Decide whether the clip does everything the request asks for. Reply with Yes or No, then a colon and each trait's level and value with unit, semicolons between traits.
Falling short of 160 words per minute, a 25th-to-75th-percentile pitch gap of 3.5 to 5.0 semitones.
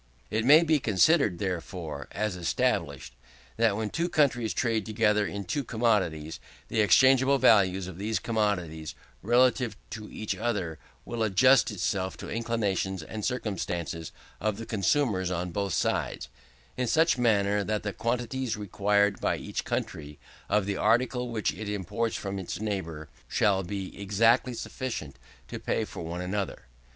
Yes: average, 150 wpm; average, 3.8 semitones